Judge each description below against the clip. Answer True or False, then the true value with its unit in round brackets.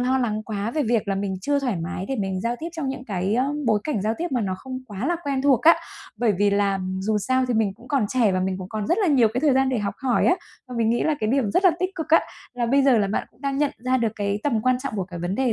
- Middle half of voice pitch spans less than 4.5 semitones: False (4.8 semitones)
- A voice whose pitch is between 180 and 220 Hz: False (235 Hz)